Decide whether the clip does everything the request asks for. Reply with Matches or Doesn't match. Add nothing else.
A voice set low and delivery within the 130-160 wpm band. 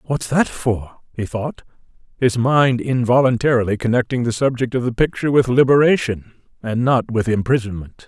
Matches